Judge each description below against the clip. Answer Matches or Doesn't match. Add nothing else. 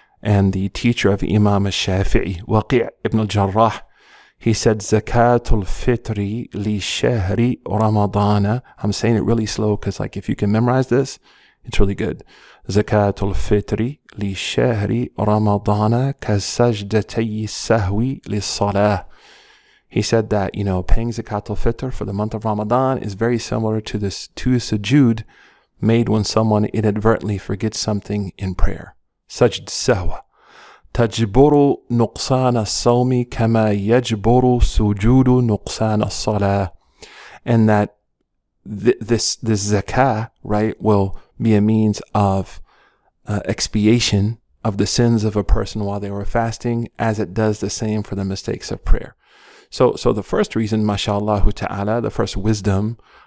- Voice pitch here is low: Matches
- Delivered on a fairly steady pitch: Matches